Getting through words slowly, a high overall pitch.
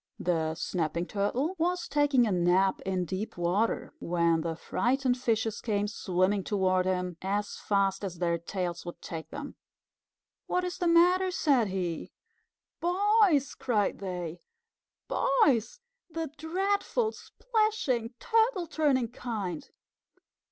Yes: slow, 125 wpm; high, 215 Hz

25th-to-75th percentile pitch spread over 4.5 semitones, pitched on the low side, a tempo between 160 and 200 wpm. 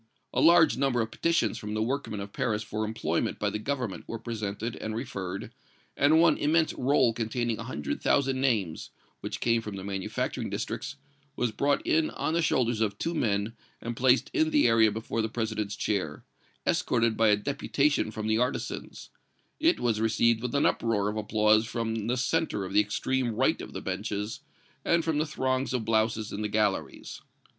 No: average, 3.7 semitones; low, 115 Hz; average, 185 wpm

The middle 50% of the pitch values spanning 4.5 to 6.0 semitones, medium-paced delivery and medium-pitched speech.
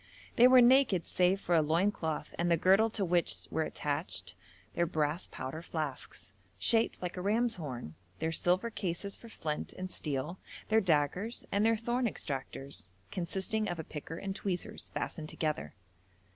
Yes: average, 5.0 semitones; average, 165 wpm; medium, 175 Hz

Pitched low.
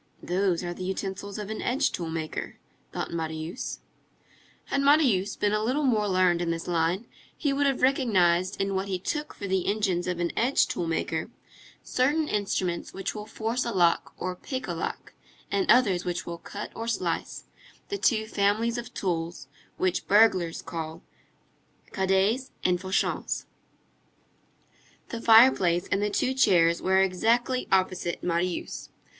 No: high, 195 Hz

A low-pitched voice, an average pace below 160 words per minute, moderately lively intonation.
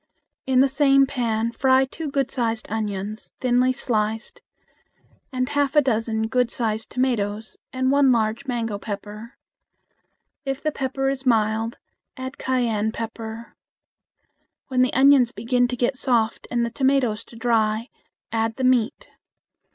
No: high, 240 Hz; average, 140 wpm; average, 3.0 semitones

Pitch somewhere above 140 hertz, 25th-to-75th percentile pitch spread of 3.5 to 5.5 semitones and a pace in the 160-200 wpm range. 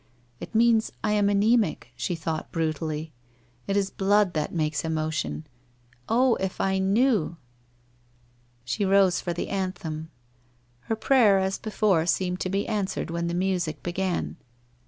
No: medium, 185 Hz; average, 4.0 semitones; average, 145 wpm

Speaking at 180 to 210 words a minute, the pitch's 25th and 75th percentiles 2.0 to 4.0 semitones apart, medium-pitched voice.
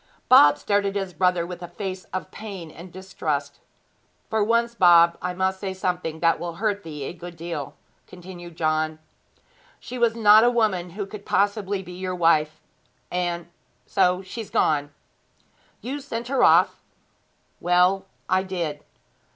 No: average, 155 wpm; average, 3.0 semitones; medium, 180 Hz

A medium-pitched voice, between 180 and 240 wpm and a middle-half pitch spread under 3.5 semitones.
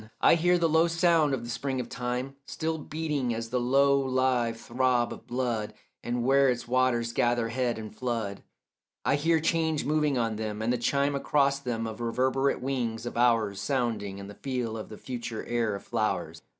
No: low, 125 Hz; average, 185 wpm; average, 3.1 semitones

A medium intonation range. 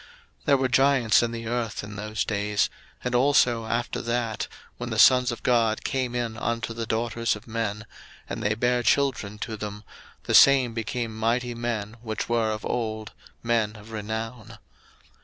No: narrow, 2.0 semitones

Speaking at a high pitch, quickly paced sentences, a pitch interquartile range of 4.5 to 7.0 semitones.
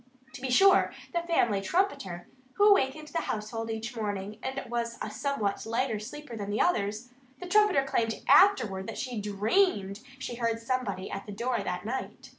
No: high, 235 Hz; average, 180 wpm; average, 5.0 semitones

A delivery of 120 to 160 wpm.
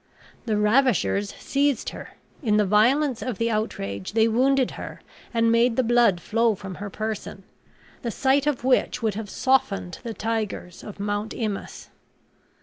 Yes: average, 155 wpm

